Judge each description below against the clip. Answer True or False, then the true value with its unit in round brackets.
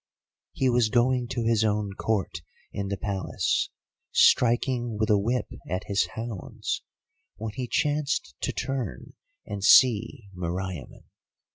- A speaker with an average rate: False (130 wpm)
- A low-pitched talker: True (110 Hz)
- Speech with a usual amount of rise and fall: True (3.7 semitones)